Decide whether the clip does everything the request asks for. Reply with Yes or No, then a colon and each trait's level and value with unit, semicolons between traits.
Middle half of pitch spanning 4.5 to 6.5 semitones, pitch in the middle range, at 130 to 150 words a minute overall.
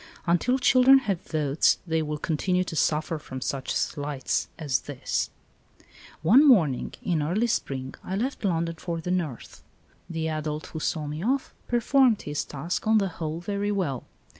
No: average, 5.2 semitones; medium, 165 Hz; average, 165 wpm